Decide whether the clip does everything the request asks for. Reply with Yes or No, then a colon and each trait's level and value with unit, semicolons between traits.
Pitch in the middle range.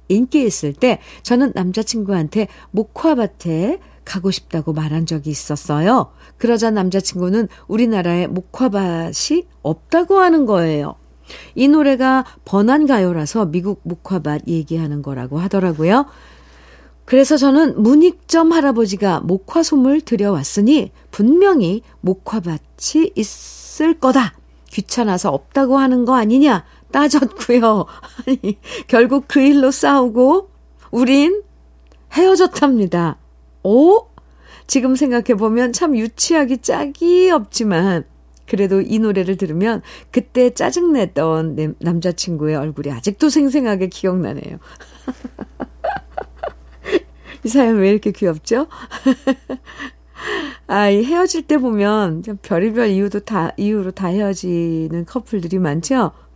No: high, 220 Hz